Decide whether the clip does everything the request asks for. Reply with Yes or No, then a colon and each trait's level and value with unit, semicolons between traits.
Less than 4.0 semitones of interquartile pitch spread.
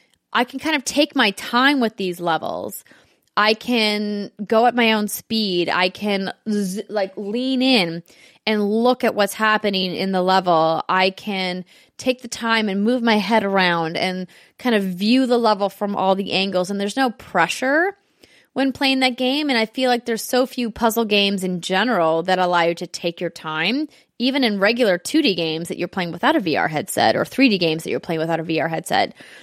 No: average, 4.8 semitones